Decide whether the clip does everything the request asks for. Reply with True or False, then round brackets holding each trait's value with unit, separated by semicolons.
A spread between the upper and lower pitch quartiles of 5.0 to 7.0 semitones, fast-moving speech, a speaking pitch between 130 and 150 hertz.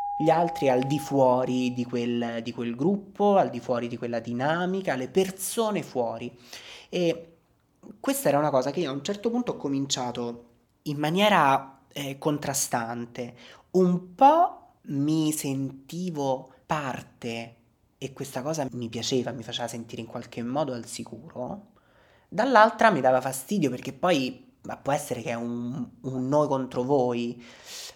False (5.3 semitones; 150 wpm; 135 Hz)